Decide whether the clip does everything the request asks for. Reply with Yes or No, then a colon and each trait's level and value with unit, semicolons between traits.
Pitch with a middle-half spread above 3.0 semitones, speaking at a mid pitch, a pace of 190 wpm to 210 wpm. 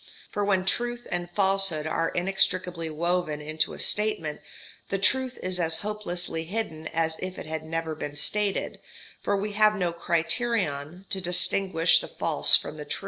No: average, 3.5 semitones; medium, 180 Hz; average, 165 wpm